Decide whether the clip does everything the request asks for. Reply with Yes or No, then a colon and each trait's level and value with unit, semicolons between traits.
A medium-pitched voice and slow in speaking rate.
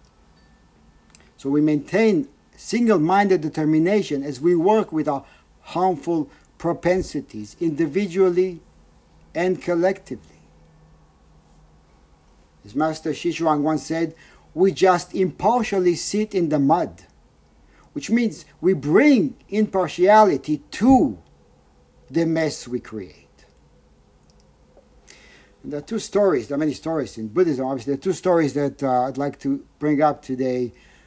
Yes: medium, 155 Hz; slow, 120 wpm